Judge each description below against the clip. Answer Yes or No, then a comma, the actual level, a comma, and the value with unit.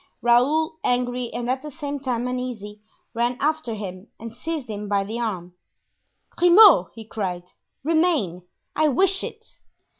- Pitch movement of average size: No, wide, 6.1 semitones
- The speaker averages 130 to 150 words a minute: Yes, average, 145 wpm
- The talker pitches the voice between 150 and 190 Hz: No, high, 245 Hz